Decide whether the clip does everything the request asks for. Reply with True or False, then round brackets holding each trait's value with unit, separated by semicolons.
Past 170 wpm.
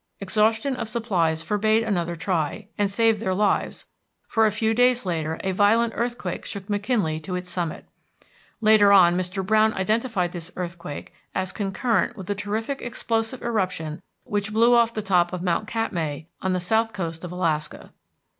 False (165 wpm)